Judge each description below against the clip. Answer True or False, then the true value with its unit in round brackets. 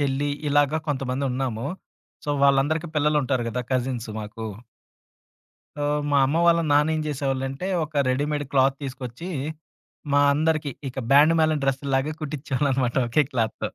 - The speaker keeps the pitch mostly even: True (2.3 semitones)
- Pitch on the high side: False (140 Hz)